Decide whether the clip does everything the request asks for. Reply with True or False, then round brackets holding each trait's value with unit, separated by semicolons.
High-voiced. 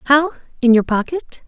True (270 Hz)